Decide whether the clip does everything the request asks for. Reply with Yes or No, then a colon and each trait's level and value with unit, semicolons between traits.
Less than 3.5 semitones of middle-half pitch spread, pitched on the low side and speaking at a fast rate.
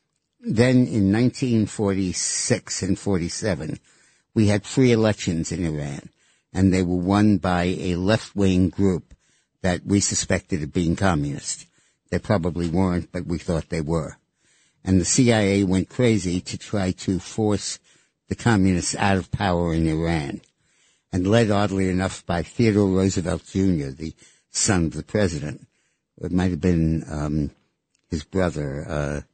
No: average, 3.0 semitones; very low, 95 Hz; average, 145 wpm